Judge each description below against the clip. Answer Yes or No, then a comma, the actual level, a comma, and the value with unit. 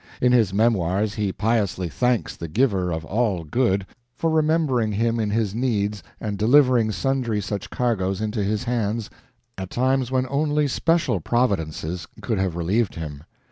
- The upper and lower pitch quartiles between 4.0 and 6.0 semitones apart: Yes, average, 4.4 semitones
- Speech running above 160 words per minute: No, average, 155 wpm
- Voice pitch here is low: Yes, low, 110 Hz